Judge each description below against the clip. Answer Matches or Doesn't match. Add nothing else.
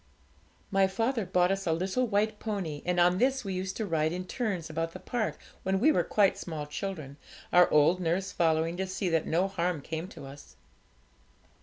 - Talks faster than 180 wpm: Matches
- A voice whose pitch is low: Doesn't match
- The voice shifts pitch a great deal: Doesn't match